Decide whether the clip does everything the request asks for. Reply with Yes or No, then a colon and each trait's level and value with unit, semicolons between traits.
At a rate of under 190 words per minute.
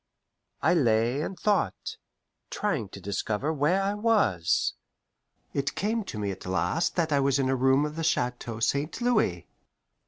Yes: average, 160 wpm